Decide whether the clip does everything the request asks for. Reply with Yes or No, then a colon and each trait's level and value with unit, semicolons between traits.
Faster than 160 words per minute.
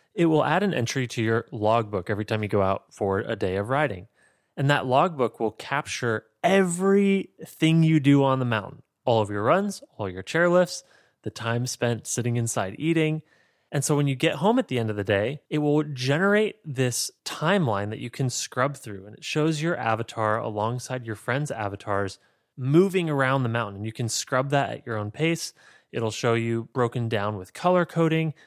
Yes: average, 200 wpm